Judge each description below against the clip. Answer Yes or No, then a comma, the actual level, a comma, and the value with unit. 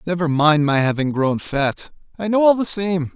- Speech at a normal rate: No, fast, 210 wpm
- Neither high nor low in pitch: Yes, medium, 165 Hz